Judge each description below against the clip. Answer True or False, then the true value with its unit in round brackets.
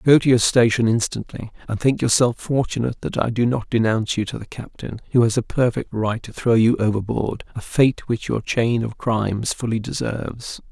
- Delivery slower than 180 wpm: False (195 wpm)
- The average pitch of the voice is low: True (115 Hz)